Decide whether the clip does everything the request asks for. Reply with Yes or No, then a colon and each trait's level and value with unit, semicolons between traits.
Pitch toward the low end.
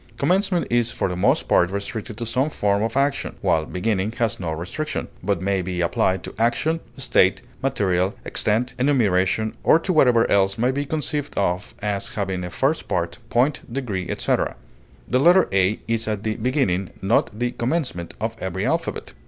Yes: low, 110 Hz